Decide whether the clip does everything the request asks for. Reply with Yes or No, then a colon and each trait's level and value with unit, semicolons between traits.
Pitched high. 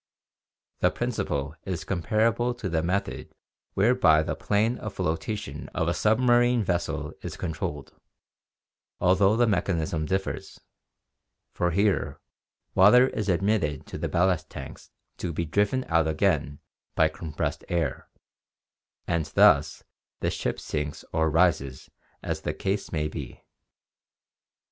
No: very low, 90 Hz